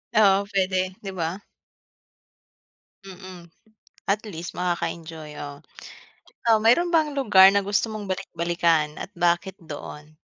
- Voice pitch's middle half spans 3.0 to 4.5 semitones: Yes, average, 3.3 semitones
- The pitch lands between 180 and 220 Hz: Yes, medium, 185 Hz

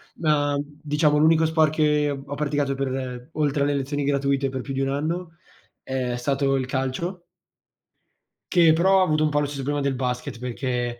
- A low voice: No, medium, 145 Hz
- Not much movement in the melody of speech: Yes, narrow, 2.3 semitones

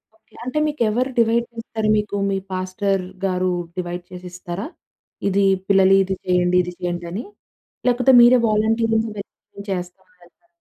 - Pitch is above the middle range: Yes, high, 195 Hz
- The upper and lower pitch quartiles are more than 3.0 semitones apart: Yes, average, 3.7 semitones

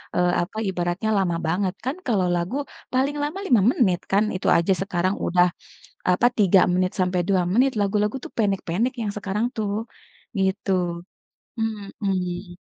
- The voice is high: Yes, high, 195 Hz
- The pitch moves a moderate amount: Yes, average, 3.1 semitones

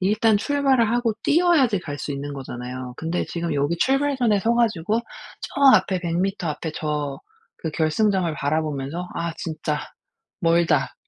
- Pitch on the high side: No, medium, 170 Hz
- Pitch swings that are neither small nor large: No, wide, 6.7 semitones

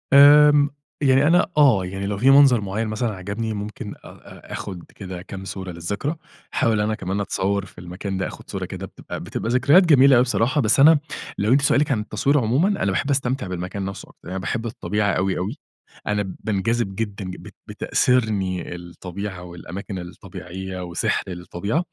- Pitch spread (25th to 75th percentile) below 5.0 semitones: No, wide, 5.4 semitones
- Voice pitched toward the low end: Yes, low, 105 Hz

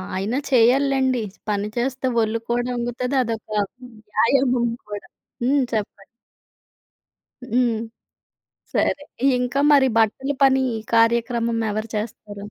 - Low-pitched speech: No, high, 235 Hz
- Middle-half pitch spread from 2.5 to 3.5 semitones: Yes, average, 2.8 semitones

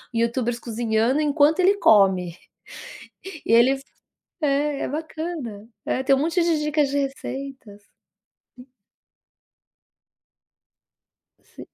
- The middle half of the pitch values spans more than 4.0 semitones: Yes, average, 4.6 semitones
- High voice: Yes, very high, 270 Hz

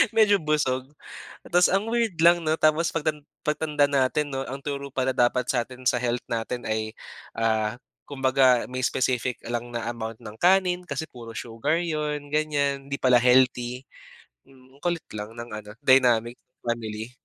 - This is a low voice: Yes, low, 130 Hz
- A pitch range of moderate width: Yes, average, 4.1 semitones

